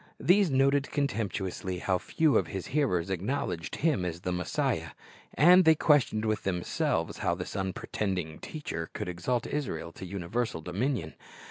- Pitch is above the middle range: No, low, 100 Hz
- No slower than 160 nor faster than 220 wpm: No, average, 145 wpm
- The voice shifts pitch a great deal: Yes, wide, 7.8 semitones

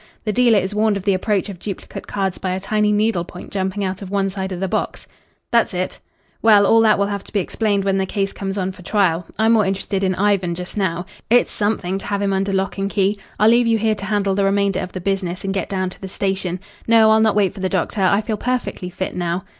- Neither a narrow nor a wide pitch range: No, narrow, 1.8 semitones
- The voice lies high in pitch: Yes, high, 195 Hz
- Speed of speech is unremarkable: No, fast, 260 wpm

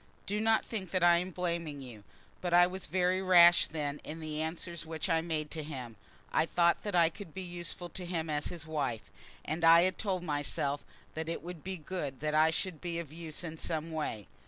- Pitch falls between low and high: Yes, medium, 165 Hz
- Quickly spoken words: Yes, fast, 220 wpm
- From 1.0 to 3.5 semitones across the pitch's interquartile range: Yes, narrow, 2.5 semitones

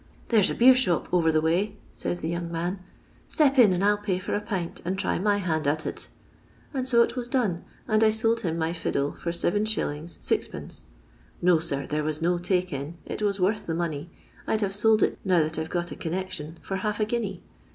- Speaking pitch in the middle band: Yes, medium, 180 Hz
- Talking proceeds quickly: Yes, fast, 235 wpm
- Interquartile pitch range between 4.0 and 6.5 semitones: Yes, average, 4.3 semitones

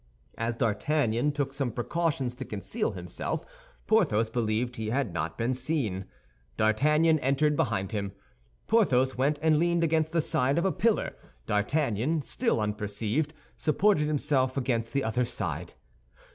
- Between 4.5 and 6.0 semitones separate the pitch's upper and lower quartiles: Yes, wide, 5.6 semitones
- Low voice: Yes, low, 130 Hz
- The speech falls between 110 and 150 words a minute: Yes, average, 140 wpm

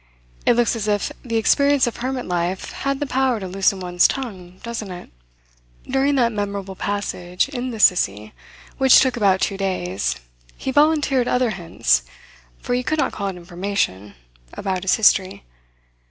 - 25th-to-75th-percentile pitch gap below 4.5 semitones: No, wide, 5.5 semitones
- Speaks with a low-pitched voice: No, high, 205 Hz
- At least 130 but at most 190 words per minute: Yes, average, 165 wpm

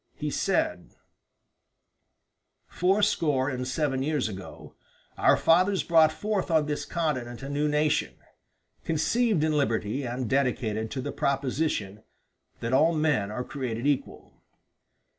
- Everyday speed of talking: No, slow, 125 wpm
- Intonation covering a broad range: No, average, 4.0 semitones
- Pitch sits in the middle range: Yes, medium, 145 Hz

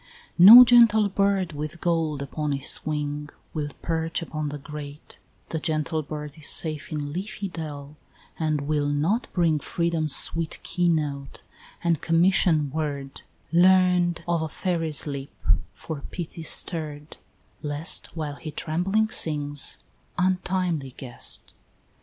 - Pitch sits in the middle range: Yes, medium, 155 Hz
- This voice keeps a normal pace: No, slow, 130 wpm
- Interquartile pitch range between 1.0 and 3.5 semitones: Yes, average, 2.8 semitones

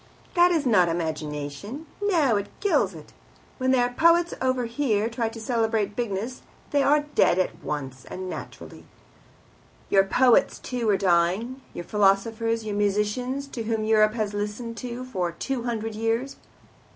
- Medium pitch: No, high, 225 Hz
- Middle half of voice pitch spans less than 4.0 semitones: No, average, 4.4 semitones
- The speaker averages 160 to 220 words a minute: No, average, 150 wpm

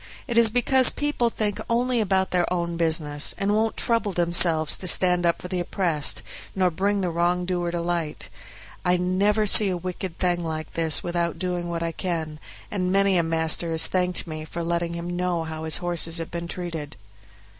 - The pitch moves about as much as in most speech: No, narrow, 2.2 semitones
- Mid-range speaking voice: Yes, medium, 175 Hz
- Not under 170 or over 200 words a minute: Yes, average, 190 wpm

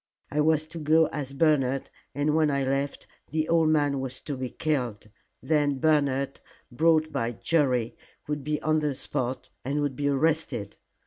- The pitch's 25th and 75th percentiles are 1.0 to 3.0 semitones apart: Yes, average, 2.7 semitones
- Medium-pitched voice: Yes, medium, 145 Hz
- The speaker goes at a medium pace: Yes, average, 170 wpm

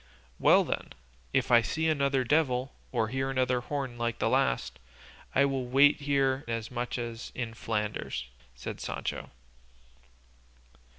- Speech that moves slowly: Yes, slow, 130 wpm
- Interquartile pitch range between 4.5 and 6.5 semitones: No, average, 2.8 semitones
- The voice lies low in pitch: Yes, low, 130 Hz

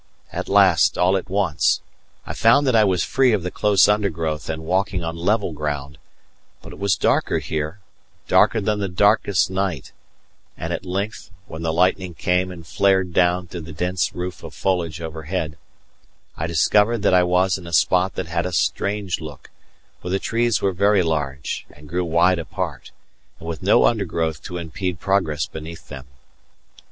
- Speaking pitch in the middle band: No, very low, 90 Hz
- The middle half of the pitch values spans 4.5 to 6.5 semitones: No, average, 3.2 semitones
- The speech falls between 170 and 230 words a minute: Yes, average, 175 wpm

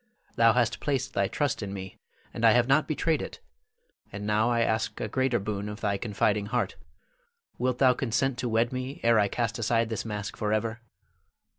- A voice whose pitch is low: Yes, low, 115 Hz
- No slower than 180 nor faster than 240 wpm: Yes, average, 190 wpm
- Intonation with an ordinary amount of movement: Yes, average, 3.0 semitones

